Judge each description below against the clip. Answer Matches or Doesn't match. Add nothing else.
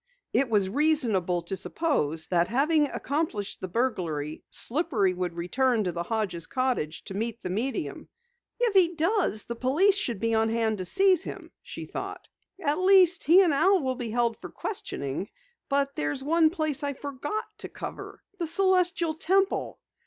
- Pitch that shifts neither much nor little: Doesn't match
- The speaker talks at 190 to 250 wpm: Doesn't match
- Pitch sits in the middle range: Doesn't match